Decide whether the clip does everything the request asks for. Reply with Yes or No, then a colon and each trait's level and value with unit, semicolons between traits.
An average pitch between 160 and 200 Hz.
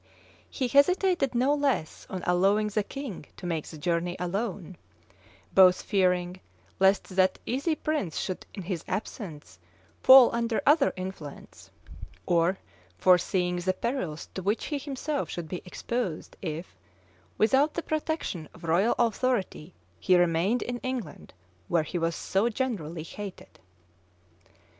Yes: high, 190 Hz